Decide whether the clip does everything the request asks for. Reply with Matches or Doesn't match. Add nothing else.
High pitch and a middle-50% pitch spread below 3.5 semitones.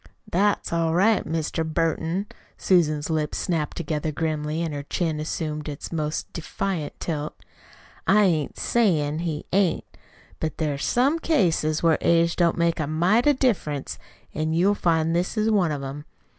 Doesn't match